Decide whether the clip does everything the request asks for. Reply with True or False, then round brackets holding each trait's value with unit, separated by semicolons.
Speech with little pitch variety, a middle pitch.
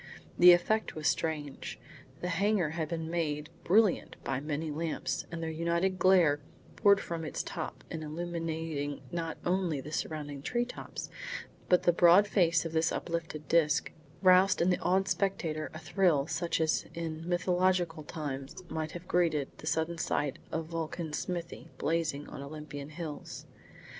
True (2.3 semitones; 165 Hz)